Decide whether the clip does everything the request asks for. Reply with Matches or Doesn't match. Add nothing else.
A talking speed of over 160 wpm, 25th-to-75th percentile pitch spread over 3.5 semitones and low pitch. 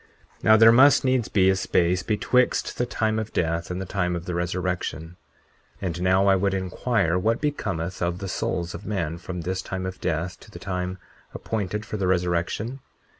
Doesn't match